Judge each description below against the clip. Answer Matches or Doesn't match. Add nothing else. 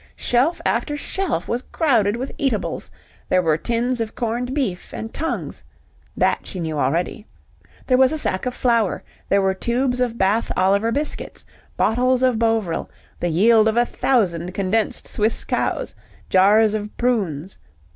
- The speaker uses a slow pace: Doesn't match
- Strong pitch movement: Doesn't match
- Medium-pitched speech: Doesn't match